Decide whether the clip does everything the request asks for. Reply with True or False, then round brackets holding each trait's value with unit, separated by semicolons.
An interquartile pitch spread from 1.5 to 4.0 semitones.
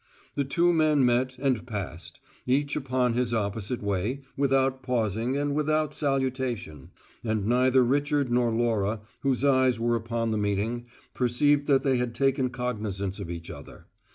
True (3.4 semitones)